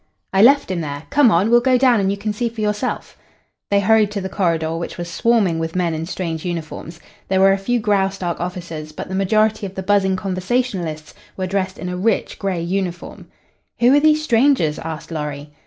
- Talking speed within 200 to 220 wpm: Yes, fast, 205 wpm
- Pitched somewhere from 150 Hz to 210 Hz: Yes, high, 190 Hz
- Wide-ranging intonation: No, average, 4.2 semitones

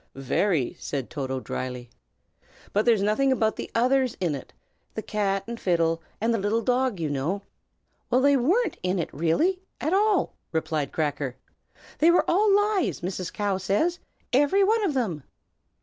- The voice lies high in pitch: Yes, high, 210 Hz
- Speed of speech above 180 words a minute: No, average, 165 wpm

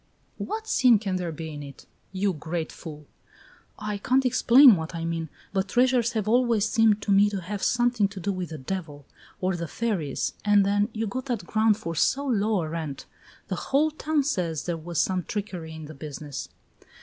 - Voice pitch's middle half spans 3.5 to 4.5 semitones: No, wide, 5.4 semitones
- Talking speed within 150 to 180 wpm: No, average, 195 wpm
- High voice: Yes, high, 195 Hz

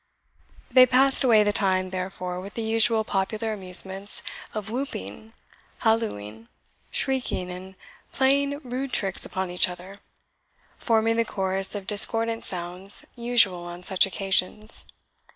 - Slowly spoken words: Yes, slow, 125 wpm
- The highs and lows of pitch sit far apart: No, average, 3.6 semitones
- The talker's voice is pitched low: No, high, 205 Hz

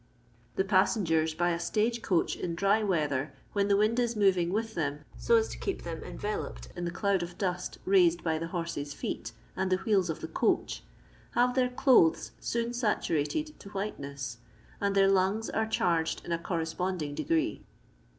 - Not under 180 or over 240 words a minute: Yes, average, 185 wpm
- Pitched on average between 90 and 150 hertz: No, medium, 185 Hz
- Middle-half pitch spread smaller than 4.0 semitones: No, average, 4.5 semitones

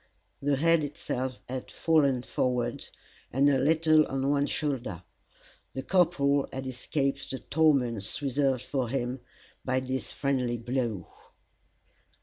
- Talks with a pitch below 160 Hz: Yes, low, 135 Hz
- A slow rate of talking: Yes, slow, 125 wpm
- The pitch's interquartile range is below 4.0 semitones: Yes, narrow, 2.4 semitones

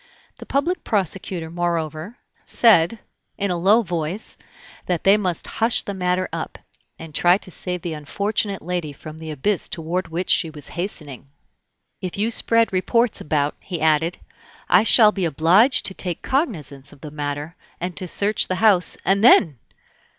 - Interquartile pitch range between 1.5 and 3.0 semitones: No, average, 4.2 semitones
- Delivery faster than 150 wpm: Yes, average, 165 wpm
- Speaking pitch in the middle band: Yes, medium, 180 Hz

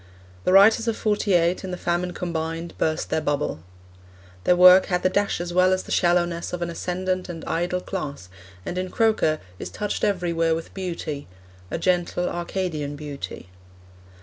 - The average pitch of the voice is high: No, medium, 175 Hz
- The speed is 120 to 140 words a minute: No, average, 170 wpm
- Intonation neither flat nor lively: No, narrow, 2.0 semitones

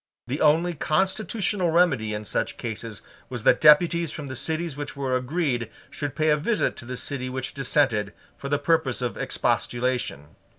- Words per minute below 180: Yes, average, 170 wpm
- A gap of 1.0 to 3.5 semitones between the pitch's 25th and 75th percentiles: No, average, 4.4 semitones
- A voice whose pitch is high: No, medium, 140 Hz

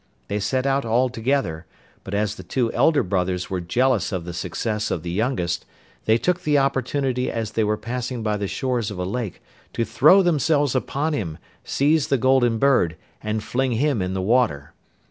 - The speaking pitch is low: Yes, low, 115 Hz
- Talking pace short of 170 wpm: No, average, 190 wpm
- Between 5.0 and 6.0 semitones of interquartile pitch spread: Yes, wide, 5.5 semitones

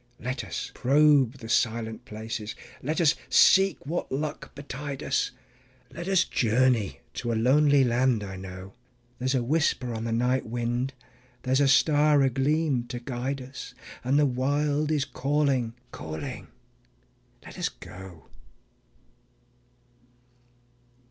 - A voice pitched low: Yes, low, 130 Hz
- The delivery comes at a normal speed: No, slow, 130 wpm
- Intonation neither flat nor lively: Yes, average, 3.7 semitones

